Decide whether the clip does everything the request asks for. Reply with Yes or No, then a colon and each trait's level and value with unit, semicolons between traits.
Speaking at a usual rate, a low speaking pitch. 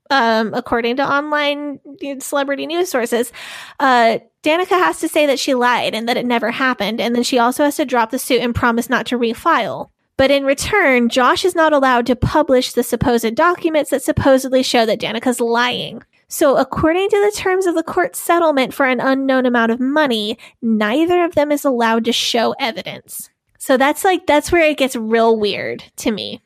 No: average, 195 wpm; very high, 265 Hz